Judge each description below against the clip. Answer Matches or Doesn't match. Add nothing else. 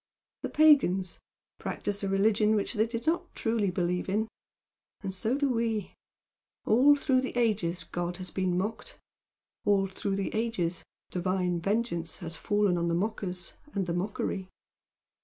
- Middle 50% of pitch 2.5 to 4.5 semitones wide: Matches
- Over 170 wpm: Doesn't match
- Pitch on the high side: Matches